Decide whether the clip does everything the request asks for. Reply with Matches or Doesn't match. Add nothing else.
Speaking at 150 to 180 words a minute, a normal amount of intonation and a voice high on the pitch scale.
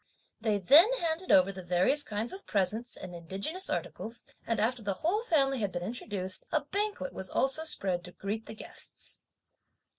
Doesn't match